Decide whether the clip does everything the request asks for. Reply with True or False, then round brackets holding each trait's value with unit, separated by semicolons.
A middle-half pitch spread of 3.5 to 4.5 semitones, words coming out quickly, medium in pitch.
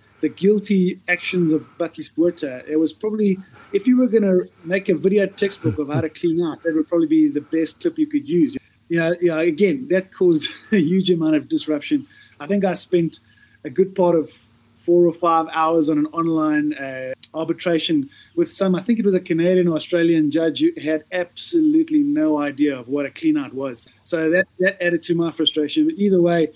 True (3.9 semitones; 210 wpm; 170 Hz)